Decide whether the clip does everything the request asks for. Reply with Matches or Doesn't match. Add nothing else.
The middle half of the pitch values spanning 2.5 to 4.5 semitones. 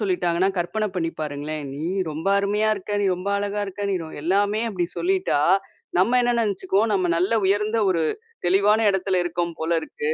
Matches